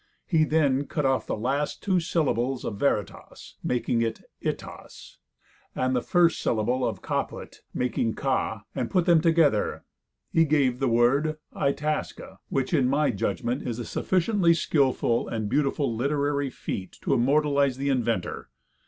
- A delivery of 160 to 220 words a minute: No, average, 145 wpm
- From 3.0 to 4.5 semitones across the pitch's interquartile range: Yes, average, 4.0 semitones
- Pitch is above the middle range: No, low, 135 Hz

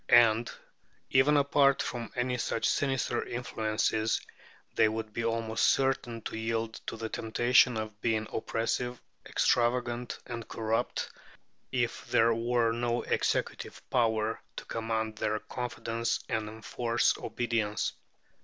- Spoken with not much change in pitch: Yes, narrow, 1.6 semitones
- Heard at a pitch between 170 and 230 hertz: No, low, 115 Hz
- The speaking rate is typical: No, slow, 120 wpm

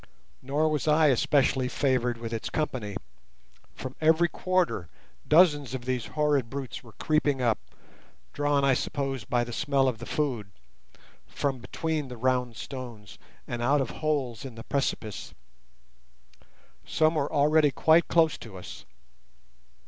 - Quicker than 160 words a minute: No, average, 140 wpm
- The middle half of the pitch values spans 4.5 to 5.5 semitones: No, average, 3.8 semitones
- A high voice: No, low, 135 Hz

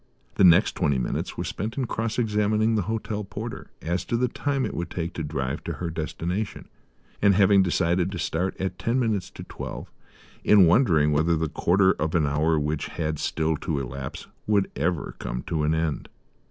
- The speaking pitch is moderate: No, very low, 85 Hz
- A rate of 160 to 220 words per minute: Yes, average, 195 wpm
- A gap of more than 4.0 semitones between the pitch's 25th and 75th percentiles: Yes, average, 5.1 semitones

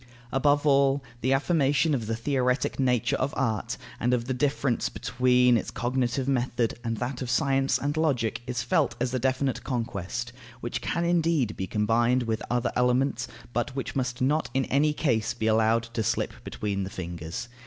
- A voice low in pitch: Yes, low, 125 Hz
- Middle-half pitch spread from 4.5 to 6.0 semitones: No, average, 2.8 semitones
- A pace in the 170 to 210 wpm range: Yes, average, 180 wpm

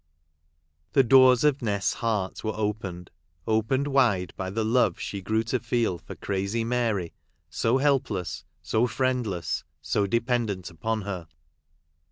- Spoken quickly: No, average, 145 wpm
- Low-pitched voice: Yes, low, 110 Hz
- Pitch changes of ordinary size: Yes, average, 4.2 semitones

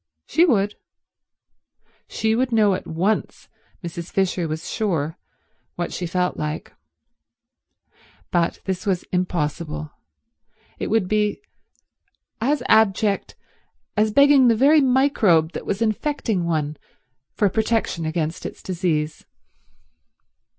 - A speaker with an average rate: No, slow, 110 wpm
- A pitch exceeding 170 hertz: Yes, high, 190 Hz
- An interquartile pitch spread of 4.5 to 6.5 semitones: Yes, average, 4.8 semitones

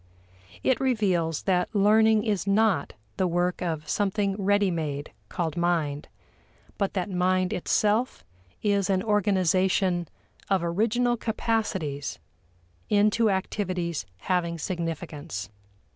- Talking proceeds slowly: Yes, slow, 105 wpm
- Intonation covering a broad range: No, average, 3.5 semitones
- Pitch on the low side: No, medium, 185 Hz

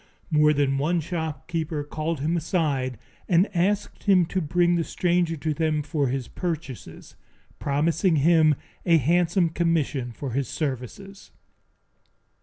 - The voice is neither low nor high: Yes, medium, 160 Hz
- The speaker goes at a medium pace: No, slow, 130 wpm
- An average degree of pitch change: Yes, average, 3.1 semitones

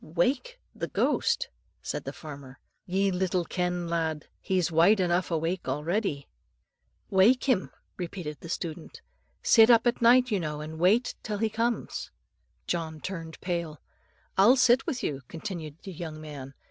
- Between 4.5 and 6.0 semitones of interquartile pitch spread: Yes, average, 5.2 semitones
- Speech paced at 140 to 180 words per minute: Yes, average, 150 wpm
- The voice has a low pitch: No, medium, 180 Hz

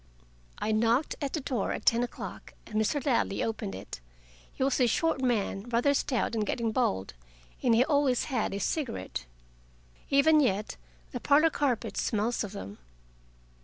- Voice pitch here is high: Yes, high, 240 Hz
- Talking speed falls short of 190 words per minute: Yes, average, 165 wpm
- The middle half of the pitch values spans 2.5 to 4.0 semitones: No, average, 4.4 semitones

